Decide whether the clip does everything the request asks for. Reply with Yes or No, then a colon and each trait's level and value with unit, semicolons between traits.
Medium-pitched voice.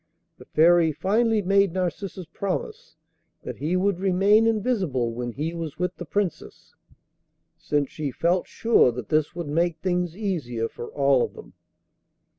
Yes: medium, 175 Hz